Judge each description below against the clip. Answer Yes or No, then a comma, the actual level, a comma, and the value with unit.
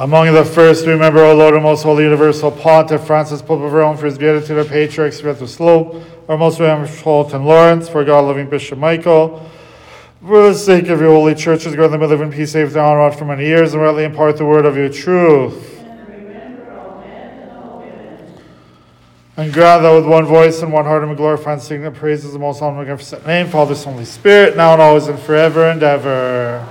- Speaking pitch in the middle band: Yes, medium, 155 Hz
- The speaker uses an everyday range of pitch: No, narrow, 1.6 semitones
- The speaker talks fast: Yes, fast, 215 wpm